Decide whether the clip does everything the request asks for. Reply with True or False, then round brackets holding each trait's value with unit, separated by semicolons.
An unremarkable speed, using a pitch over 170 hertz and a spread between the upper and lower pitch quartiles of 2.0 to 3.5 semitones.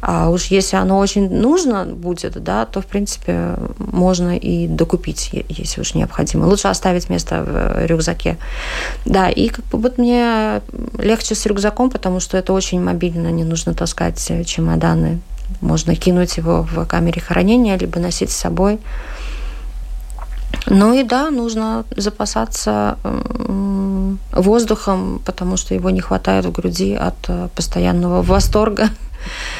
False (135 wpm; 185 Hz; 4.6 semitones)